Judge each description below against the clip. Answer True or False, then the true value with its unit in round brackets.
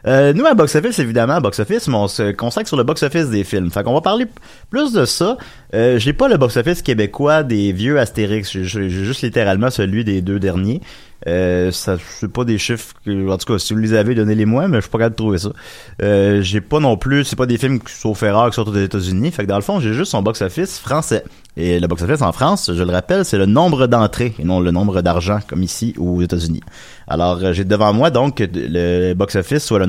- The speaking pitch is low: True (105 Hz)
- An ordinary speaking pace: False (255 wpm)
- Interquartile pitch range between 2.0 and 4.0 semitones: False (4.4 semitones)